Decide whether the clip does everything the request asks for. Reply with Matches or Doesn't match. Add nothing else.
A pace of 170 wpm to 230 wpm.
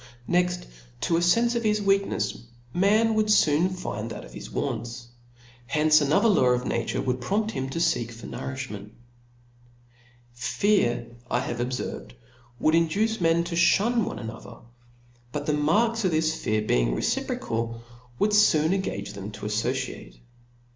Doesn't match